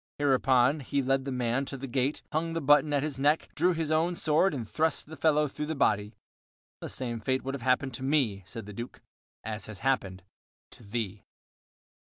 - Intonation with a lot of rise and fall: No, average, 4.1 semitones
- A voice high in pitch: No, low, 135 Hz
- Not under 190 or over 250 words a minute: Yes, fast, 205 wpm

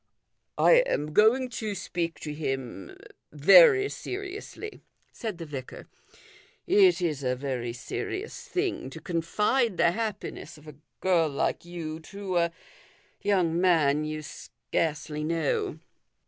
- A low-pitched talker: No, medium, 175 Hz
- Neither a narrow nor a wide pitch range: No, wide, 9.0 semitones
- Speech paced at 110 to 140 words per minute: Yes, slow, 135 wpm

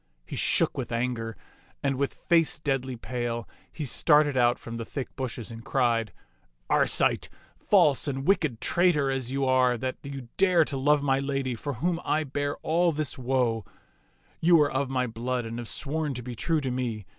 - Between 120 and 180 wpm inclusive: No, average, 190 wpm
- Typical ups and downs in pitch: Yes, average, 3.3 semitones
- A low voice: Yes, low, 130 Hz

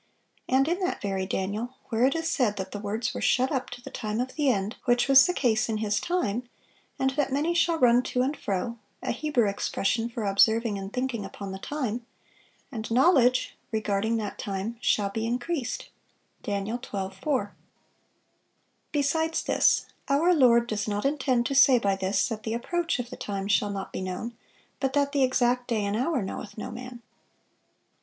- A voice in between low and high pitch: No, high, 240 Hz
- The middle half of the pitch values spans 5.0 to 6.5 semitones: No, average, 4.3 semitones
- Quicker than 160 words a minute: Yes, average, 185 wpm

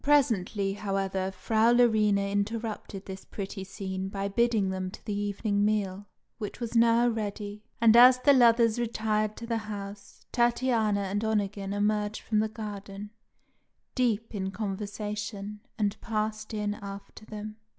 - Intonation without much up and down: Yes, narrow, 2.0 semitones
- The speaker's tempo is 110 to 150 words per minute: Yes, average, 140 wpm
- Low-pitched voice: No, high, 210 Hz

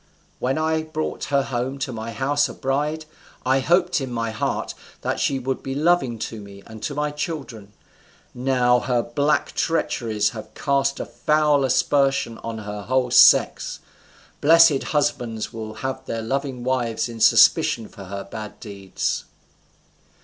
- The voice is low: Yes, low, 130 Hz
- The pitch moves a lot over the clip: No, average, 4.1 semitones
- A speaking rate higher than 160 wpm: No, average, 155 wpm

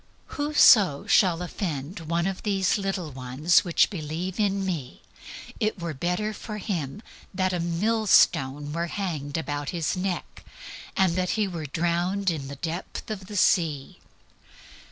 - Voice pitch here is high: No, medium, 175 Hz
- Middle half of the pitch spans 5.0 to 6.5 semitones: No, average, 3.9 semitones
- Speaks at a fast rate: No, average, 145 wpm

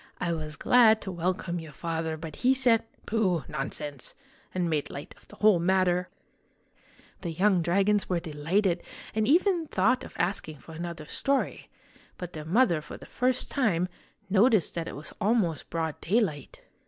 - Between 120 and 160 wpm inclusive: No, average, 180 wpm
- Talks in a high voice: No, medium, 180 Hz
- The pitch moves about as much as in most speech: Yes, average, 5.0 semitones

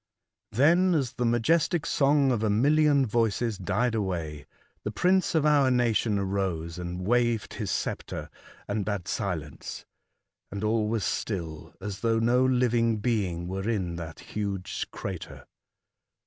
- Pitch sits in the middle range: No, low, 110 Hz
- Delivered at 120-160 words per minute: Yes, average, 140 wpm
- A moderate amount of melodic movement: Yes, average, 4.5 semitones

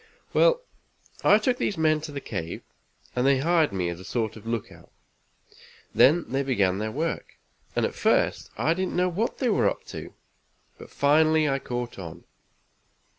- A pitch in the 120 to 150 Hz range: Yes, medium, 140 Hz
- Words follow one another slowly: No, average, 175 wpm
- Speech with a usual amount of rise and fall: No, wide, 6.7 semitones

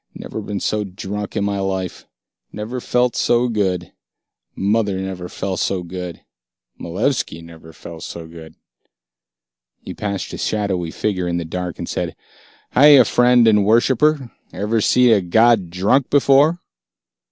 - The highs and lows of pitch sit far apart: No, average, 4.7 semitones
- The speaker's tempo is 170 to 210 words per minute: No, average, 140 wpm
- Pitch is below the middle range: Yes, low, 100 Hz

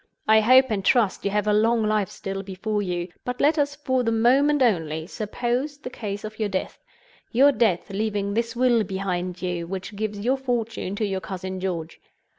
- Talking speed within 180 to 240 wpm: Yes, average, 190 wpm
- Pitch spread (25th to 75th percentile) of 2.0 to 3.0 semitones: No, average, 4.2 semitones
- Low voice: No, high, 215 Hz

